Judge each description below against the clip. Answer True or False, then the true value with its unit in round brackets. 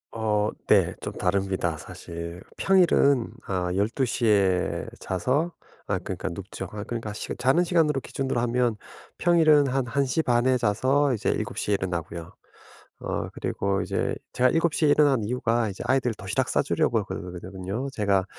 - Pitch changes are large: True (5.7 semitones)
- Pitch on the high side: False (115 Hz)